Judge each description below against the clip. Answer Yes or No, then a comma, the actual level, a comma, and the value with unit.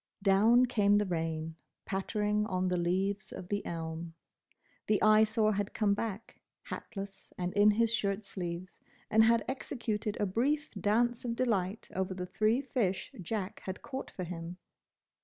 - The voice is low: No, high, 205 Hz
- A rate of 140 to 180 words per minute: Yes, average, 155 wpm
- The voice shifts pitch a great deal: No, average, 3.3 semitones